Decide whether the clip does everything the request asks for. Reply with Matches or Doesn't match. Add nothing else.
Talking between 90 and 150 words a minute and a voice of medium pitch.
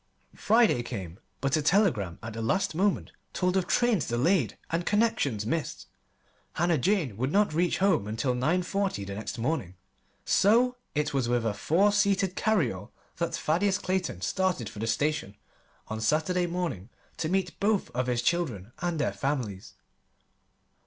Doesn't match